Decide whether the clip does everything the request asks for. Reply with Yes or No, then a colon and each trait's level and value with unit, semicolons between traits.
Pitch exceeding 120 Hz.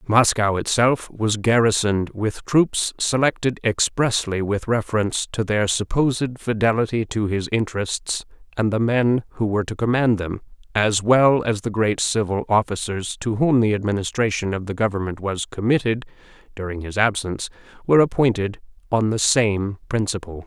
No: low, 110 Hz